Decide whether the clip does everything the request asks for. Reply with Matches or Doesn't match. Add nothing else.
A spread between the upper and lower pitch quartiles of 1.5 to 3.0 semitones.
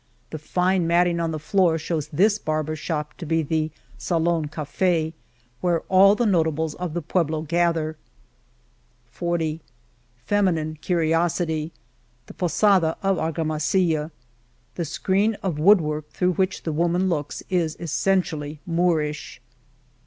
Matches